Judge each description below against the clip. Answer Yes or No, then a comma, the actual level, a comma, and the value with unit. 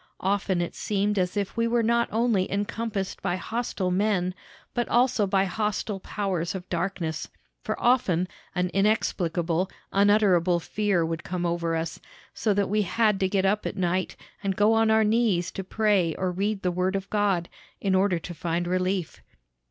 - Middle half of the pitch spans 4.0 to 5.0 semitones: No, average, 2.8 semitones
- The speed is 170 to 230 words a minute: Yes, average, 175 wpm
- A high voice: Yes, high, 195 Hz